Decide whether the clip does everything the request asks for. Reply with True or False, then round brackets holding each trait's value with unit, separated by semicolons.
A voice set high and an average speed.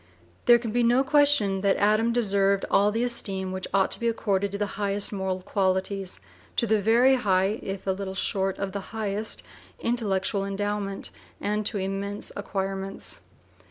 True (200 Hz; 160 wpm)